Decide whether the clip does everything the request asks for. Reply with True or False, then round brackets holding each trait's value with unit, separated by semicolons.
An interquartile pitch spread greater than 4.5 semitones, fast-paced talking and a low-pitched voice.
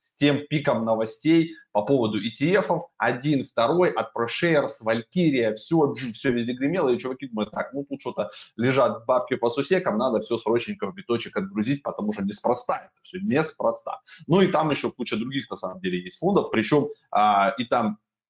True (5.3 semitones; 175 wpm; 130 Hz)